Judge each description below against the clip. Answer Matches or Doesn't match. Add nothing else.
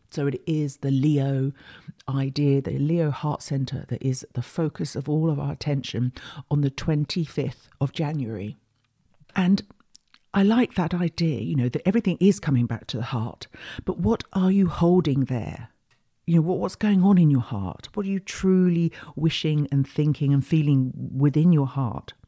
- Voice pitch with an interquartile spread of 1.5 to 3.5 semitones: Doesn't match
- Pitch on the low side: Doesn't match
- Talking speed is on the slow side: Doesn't match